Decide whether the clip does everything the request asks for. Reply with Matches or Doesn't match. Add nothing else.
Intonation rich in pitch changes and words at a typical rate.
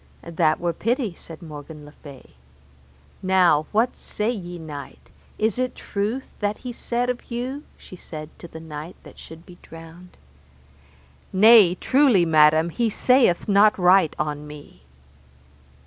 Matches